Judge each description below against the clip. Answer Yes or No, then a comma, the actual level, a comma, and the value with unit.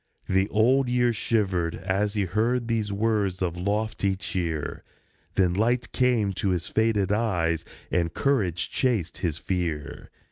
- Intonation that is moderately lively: Yes, average, 4.1 semitones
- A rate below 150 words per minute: Yes, average, 140 wpm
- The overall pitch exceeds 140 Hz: No, low, 100 Hz